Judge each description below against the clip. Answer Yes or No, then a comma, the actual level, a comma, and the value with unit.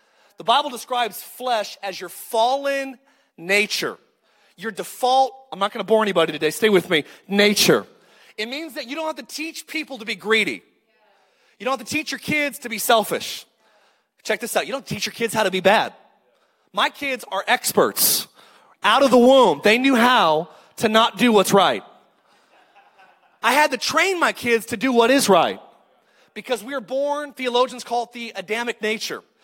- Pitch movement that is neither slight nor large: Yes, average, 4.4 semitones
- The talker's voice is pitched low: No, high, 235 Hz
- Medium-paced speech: Yes, average, 190 wpm